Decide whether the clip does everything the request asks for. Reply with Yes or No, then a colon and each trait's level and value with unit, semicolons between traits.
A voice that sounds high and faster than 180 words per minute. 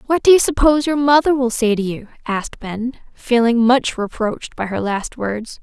Yes: high, 240 Hz; fast, 205 wpm